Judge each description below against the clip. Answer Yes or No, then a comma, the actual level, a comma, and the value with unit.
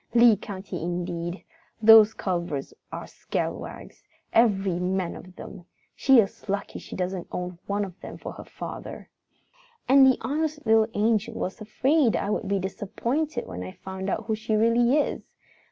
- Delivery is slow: No, average, 160 wpm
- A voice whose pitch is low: No, high, 205 Hz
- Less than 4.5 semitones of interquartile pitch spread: Yes, average, 4.1 semitones